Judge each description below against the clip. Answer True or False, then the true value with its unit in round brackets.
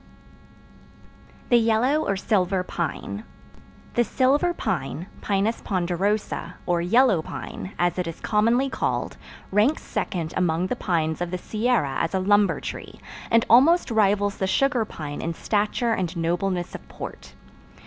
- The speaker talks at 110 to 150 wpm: True (140 wpm)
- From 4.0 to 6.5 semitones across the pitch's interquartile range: True (4.6 semitones)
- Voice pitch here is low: False (200 Hz)